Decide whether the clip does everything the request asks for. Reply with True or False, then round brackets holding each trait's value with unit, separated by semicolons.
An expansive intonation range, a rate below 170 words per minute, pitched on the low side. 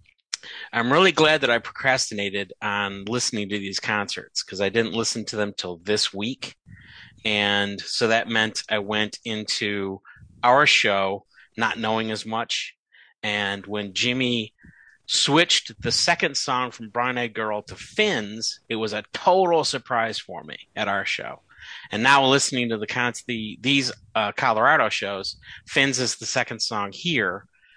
False (3.0 semitones; 160 wpm; 110 Hz)